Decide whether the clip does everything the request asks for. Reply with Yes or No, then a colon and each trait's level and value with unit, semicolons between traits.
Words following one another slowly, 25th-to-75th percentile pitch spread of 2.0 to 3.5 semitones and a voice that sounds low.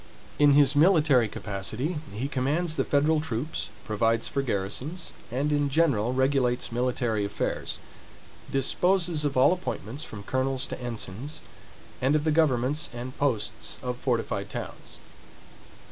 No: slow, 130 wpm; average, 4.1 semitones; low, 130 Hz